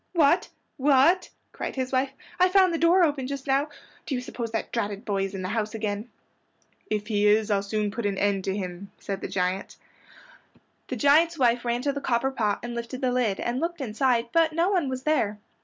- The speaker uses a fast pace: Yes, fast, 220 wpm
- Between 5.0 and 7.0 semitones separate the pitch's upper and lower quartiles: Yes, average, 5.3 semitones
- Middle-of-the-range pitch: No, high, 240 Hz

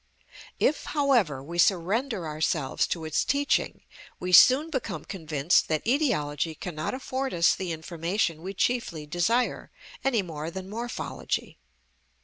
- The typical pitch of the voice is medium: Yes, medium, 180 Hz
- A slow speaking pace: Yes, slow, 130 wpm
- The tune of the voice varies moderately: No, wide, 7.2 semitones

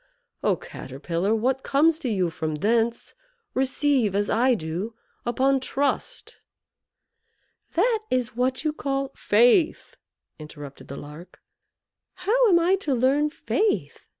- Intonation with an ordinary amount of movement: No, wide, 6.7 semitones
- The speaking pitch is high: Yes, very high, 255 Hz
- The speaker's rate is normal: No, slow, 125 wpm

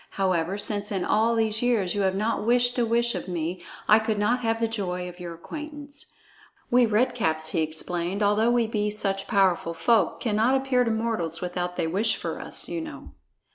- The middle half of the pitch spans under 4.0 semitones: No, average, 4.5 semitones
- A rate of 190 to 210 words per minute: Yes, average, 200 wpm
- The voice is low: No, high, 210 Hz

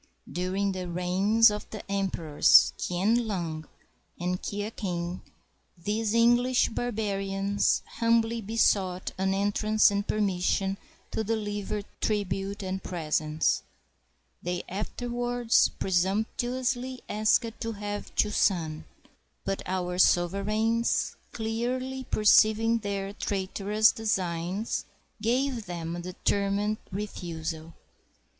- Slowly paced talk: Yes, slow, 100 wpm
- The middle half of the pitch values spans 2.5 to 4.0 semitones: Yes, average, 3.4 semitones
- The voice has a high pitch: Yes, high, 205 Hz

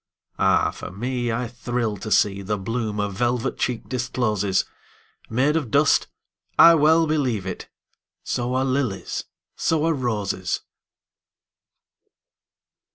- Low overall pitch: Yes, low, 120 Hz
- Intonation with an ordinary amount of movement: Yes, average, 4.0 semitones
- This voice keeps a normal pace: No, slow, 100 wpm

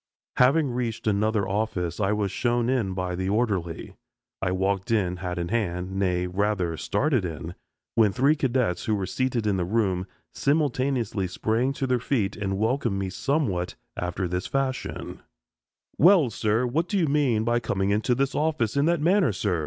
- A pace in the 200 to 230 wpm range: No, average, 175 wpm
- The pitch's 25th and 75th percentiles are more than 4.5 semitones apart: Yes, wide, 5.5 semitones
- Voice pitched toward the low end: Yes, low, 110 Hz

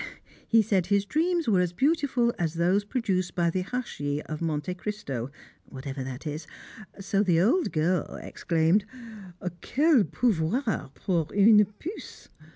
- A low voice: No, medium, 185 Hz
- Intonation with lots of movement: Yes, wide, 5.9 semitones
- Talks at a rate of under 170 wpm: Yes, average, 140 wpm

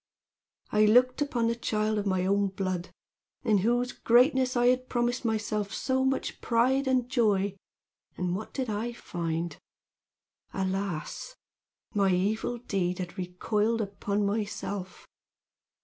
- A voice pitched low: No, high, 215 Hz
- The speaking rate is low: Yes, slow, 130 wpm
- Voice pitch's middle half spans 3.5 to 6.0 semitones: Yes, average, 3.9 semitones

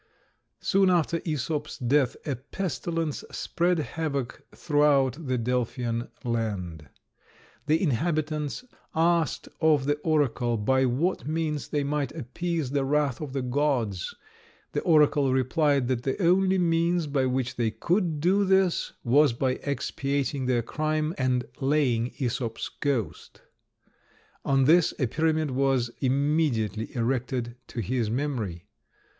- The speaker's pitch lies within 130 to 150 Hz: Yes, medium, 140 Hz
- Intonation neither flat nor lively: Yes, average, 4.0 semitones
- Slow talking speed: Yes, slow, 125 wpm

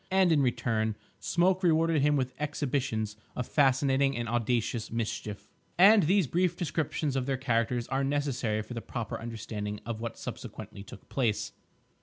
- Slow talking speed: No, average, 155 wpm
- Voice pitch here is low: Yes, low, 130 Hz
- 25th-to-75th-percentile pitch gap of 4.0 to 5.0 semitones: Yes, average, 4.5 semitones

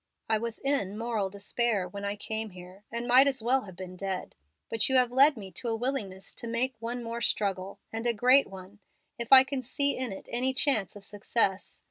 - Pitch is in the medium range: No, high, 225 Hz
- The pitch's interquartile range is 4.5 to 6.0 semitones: No, average, 4.1 semitones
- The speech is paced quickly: Yes, fast, 215 wpm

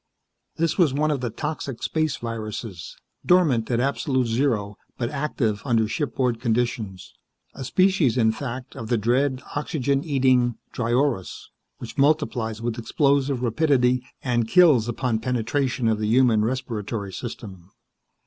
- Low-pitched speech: Yes, low, 125 Hz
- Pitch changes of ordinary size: Yes, average, 3.7 semitones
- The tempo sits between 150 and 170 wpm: No, slow, 135 wpm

